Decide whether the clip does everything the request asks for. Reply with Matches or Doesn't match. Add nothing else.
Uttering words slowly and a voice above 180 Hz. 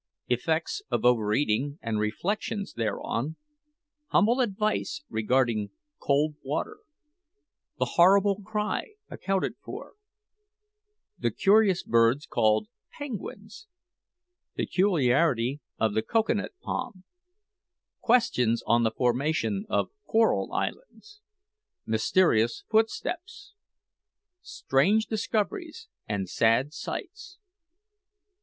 Doesn't match